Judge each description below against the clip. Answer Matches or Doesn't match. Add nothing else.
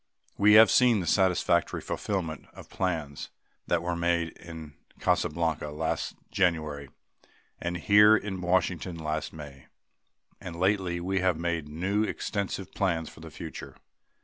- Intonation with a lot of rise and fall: Doesn't match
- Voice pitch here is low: Matches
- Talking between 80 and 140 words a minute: Matches